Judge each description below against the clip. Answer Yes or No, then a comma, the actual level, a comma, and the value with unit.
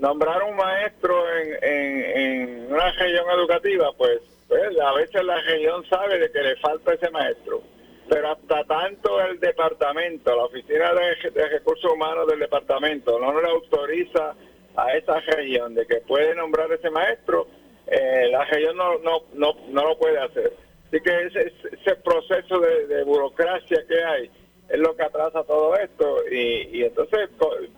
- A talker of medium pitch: No, high, 235 Hz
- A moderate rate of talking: Yes, average, 165 wpm